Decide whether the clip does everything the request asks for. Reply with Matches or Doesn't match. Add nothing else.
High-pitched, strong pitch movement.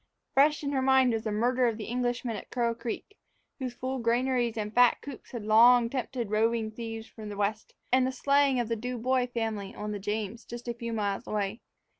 Doesn't match